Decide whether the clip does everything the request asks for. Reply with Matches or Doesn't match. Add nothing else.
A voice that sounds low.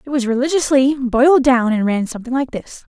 Doesn't match